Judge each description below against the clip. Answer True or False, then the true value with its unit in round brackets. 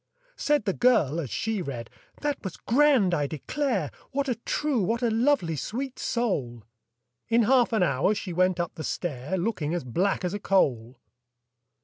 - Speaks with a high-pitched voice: True (195 Hz)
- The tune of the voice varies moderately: False (7.4 semitones)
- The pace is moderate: True (170 wpm)